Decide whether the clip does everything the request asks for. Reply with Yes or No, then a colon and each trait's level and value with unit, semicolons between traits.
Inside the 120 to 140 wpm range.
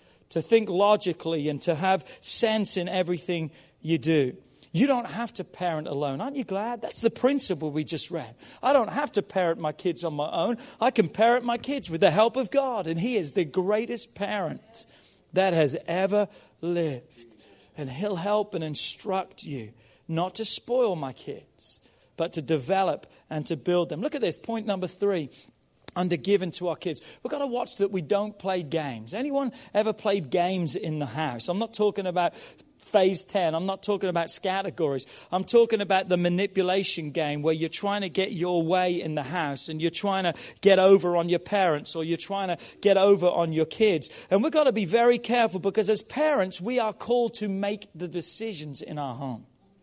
No: average, 200 wpm